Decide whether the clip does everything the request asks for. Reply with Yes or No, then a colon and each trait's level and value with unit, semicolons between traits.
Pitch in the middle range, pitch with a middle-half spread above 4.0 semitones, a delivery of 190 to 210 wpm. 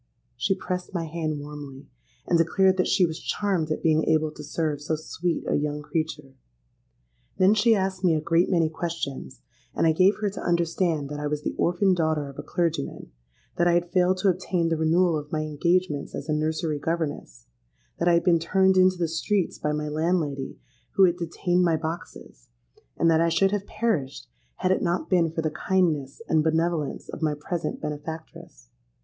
No: medium, 165 Hz; average, 3.0 semitones; average, 195 wpm